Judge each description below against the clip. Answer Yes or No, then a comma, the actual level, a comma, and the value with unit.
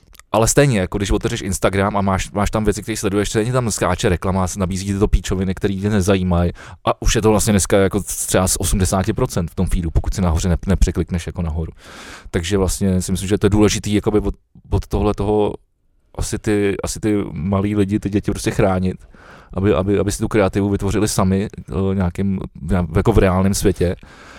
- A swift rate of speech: Yes, fast, 200 wpm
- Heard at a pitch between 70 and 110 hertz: Yes, low, 100 Hz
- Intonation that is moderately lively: No, narrow, 2.1 semitones